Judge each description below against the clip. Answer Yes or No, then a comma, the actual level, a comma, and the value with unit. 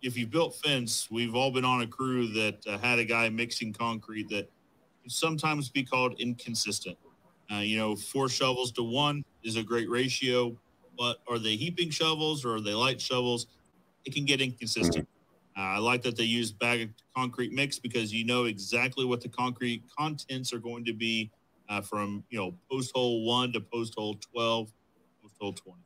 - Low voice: Yes, low, 120 Hz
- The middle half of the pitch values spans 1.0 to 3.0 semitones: Yes, narrow, 2.6 semitones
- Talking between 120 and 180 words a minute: No, average, 195 wpm